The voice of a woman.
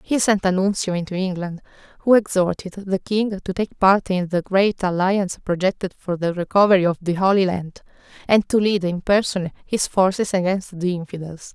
Yes: female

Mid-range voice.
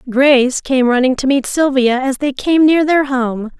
No: very high, 265 Hz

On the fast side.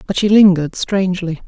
No: average, 165 wpm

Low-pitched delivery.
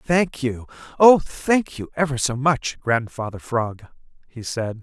Yes: low, 130 Hz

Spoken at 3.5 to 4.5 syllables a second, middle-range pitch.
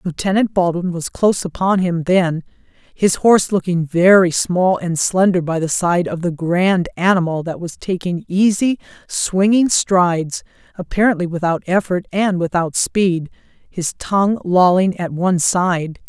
Yes: 4.4 syllables/s; medium, 180 Hz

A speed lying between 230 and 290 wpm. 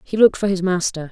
Yes: fast, 270 wpm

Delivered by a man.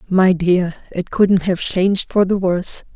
No: female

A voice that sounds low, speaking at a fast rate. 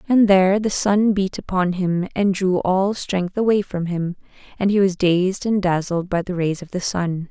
No: high, 190 Hz; fast, 215 wpm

